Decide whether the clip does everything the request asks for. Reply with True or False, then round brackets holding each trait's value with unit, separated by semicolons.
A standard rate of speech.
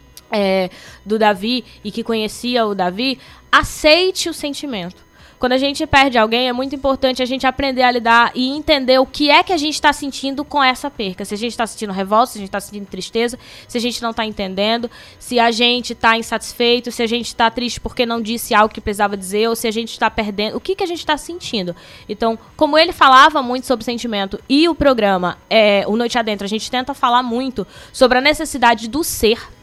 False (215 wpm)